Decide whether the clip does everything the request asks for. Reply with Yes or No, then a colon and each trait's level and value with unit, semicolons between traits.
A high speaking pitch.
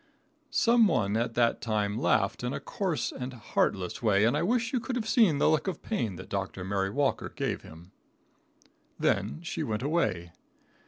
No: low, 120 Hz